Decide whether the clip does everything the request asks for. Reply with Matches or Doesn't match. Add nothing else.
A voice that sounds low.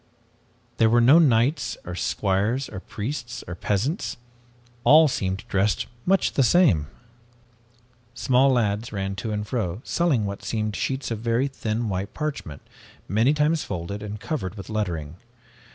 Matches